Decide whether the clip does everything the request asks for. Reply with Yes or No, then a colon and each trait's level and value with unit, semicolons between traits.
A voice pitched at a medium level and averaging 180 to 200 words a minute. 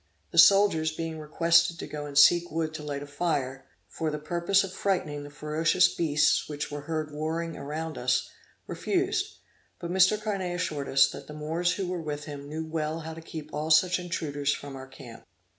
Yes: medium, 155 Hz; average, 195 wpm